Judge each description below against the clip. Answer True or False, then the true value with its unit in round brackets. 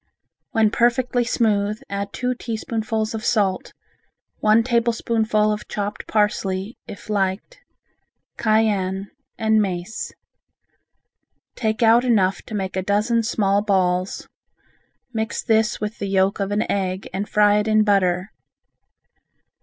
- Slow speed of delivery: True (120 wpm)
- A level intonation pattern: True (2.1 semitones)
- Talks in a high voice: True (210 Hz)